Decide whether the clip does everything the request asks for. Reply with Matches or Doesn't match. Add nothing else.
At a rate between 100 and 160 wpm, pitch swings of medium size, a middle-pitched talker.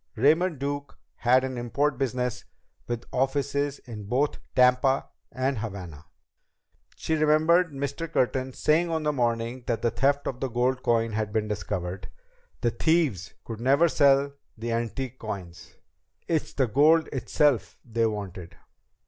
Doesn't match